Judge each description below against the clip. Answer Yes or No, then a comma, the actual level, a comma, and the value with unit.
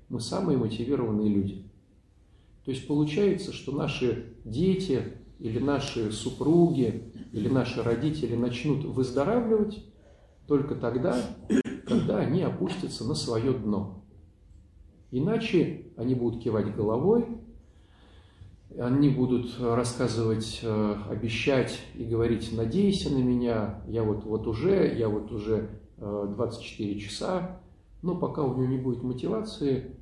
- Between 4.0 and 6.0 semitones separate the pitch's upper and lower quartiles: Yes, average, 4.8 semitones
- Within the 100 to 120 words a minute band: Yes, slow, 110 wpm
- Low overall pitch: Yes, low, 120 Hz